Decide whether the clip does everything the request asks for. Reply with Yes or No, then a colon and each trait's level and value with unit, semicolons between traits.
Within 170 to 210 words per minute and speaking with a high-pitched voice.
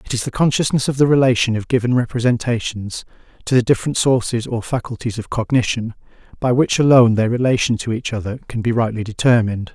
No: average, 185 wpm; low, 120 Hz